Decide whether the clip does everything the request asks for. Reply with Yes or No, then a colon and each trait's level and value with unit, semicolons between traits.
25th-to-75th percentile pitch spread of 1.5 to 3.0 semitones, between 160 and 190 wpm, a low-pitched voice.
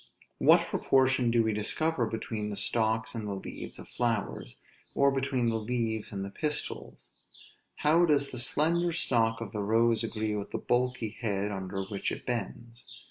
No: average, 3.4 semitones; average, 170 wpm; low, 115 Hz